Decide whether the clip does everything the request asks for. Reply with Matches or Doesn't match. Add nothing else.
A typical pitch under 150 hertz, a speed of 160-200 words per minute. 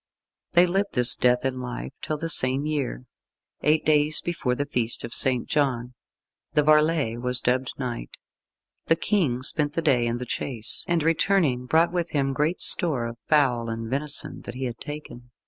Matches